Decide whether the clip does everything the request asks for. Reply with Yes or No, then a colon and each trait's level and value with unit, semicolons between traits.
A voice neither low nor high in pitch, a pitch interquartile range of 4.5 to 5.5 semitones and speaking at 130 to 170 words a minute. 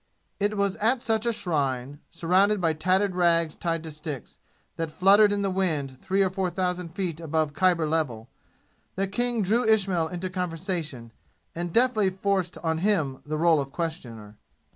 No: medium, 175 Hz; average, 3.8 semitones; average, 165 wpm